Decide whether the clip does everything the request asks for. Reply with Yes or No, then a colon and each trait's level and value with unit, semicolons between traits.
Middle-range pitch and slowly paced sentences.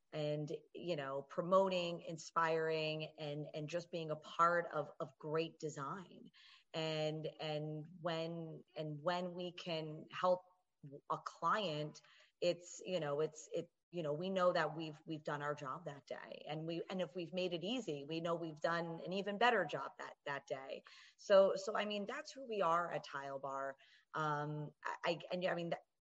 No: medium, 165 Hz; average, 180 wpm